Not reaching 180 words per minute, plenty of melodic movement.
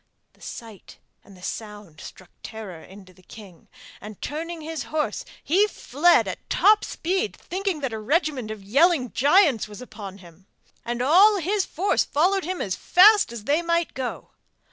Yes: average, 165 wpm; wide, 8.8 semitones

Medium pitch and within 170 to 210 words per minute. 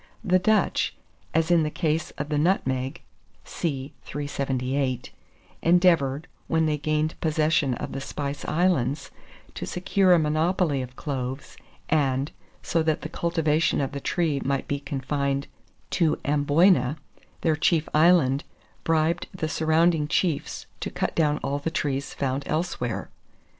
No: medium, 150 Hz; slow, 135 wpm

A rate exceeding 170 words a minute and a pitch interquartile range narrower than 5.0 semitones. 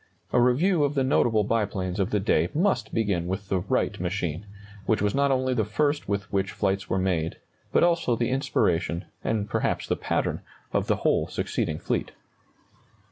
No: average, 180 wpm; wide, 5.5 semitones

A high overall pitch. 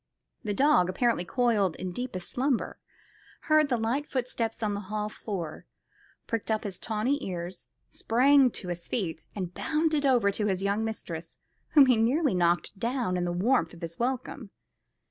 Yes: high, 220 Hz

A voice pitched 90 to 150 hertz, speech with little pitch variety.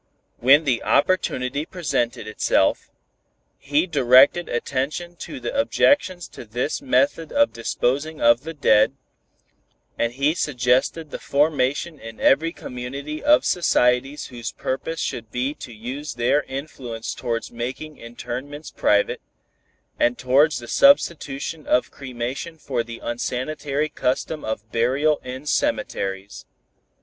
No: low, 135 Hz; average, 4.2 semitones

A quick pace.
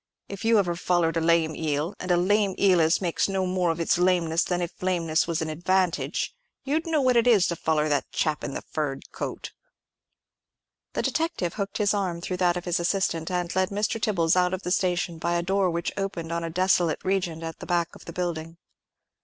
Yes: fast, 210 wpm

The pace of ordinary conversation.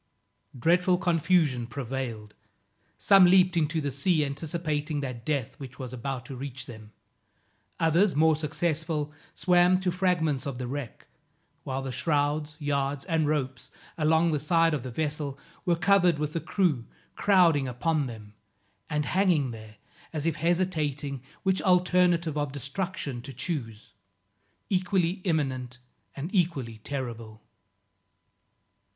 No: slow, 130 wpm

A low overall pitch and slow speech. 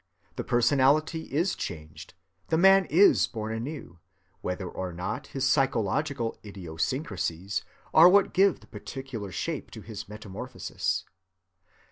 Yes: low, 120 Hz; slow, 120 wpm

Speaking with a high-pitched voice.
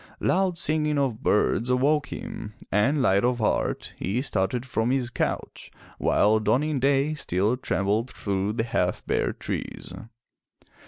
No: low, 125 Hz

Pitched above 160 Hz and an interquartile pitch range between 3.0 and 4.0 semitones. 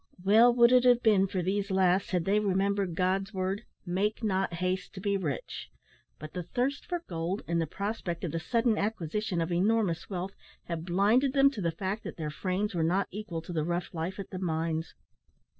Yes: high, 190 Hz; average, 3.5 semitones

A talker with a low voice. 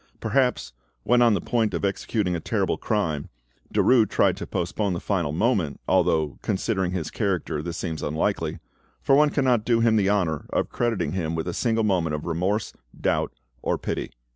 Yes: very low, 95 Hz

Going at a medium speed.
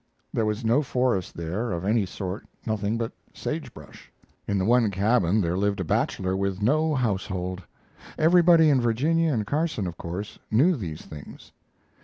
Yes: average, 165 wpm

